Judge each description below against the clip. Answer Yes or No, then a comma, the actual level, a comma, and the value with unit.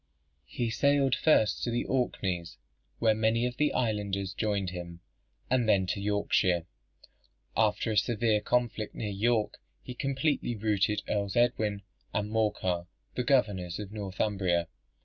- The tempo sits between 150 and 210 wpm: No, slow, 135 wpm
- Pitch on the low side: Yes, low, 105 Hz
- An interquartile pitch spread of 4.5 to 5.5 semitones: No, average, 3.5 semitones